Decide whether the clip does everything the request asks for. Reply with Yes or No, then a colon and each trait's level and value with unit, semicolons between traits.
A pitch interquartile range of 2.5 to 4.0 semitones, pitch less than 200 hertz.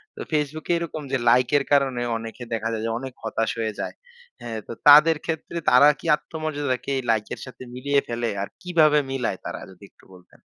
No: average, 4.7 semitones; low, 135 Hz